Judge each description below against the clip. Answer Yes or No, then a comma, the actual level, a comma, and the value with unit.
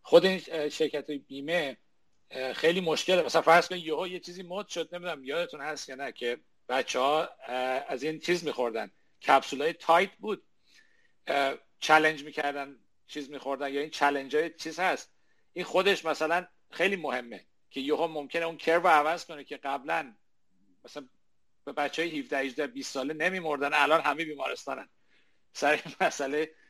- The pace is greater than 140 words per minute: Yes, fast, 155 wpm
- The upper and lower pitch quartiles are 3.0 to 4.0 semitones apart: Yes, average, 3.6 semitones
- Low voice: No, medium, 155 Hz